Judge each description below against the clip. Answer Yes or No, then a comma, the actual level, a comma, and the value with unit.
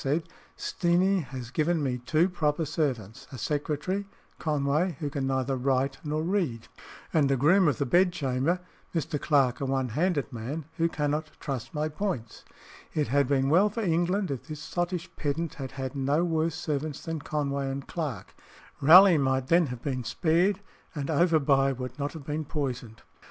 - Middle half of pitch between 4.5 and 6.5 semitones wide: No, average, 3.7 semitones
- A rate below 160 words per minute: No, average, 170 wpm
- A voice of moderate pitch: Yes, medium, 150 Hz